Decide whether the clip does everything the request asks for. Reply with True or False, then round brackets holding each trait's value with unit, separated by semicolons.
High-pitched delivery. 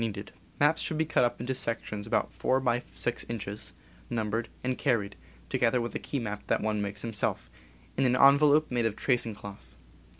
False (120 Hz)